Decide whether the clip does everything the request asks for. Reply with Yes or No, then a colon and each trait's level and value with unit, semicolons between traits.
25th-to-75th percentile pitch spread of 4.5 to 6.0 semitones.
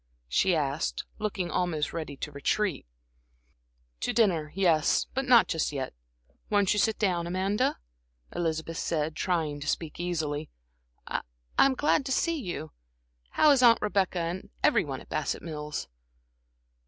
Yes: average, 5.2 semitones